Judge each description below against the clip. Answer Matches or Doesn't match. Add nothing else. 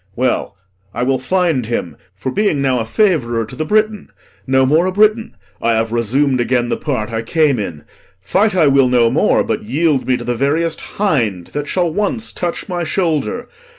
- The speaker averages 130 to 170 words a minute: Doesn't match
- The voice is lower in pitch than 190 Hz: Matches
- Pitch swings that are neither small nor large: Doesn't match